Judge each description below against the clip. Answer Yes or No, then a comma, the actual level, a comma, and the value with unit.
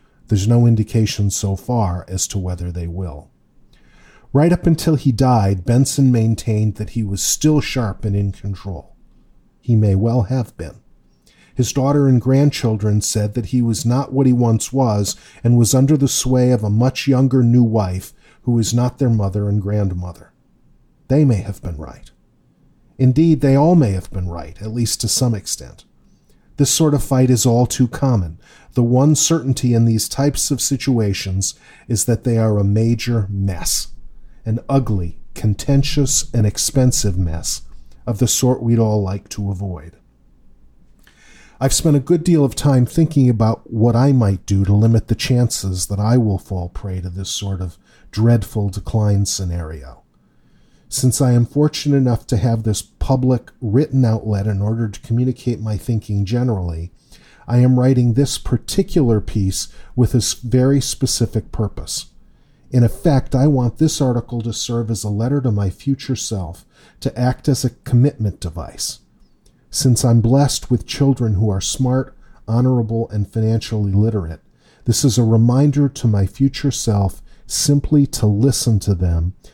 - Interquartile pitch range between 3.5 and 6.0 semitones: Yes, average, 4.4 semitones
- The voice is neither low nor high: No, low, 115 Hz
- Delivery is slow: No, average, 165 wpm